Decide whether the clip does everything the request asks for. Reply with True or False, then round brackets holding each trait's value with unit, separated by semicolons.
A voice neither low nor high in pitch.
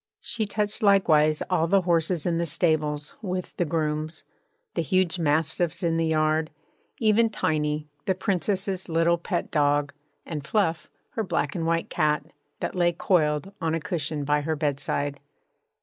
True (165 Hz)